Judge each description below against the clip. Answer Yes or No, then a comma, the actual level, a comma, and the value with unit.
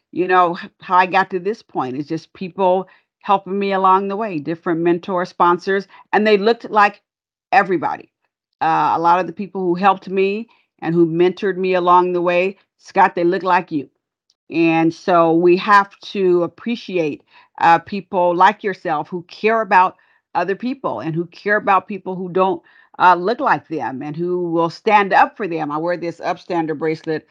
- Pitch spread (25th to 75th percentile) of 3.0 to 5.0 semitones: No, narrow, 2.5 semitones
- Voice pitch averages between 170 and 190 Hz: Yes, medium, 185 Hz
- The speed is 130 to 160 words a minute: No, average, 180 wpm